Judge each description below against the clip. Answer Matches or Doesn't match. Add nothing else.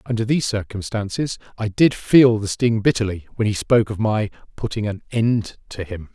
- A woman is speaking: Doesn't match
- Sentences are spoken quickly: Doesn't match